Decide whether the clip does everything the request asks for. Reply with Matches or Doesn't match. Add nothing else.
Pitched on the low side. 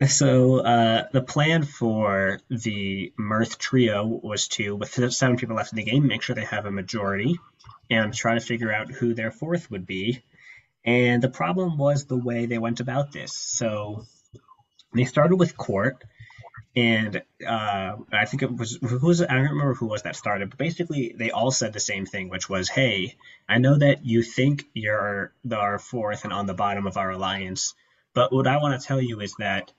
Matches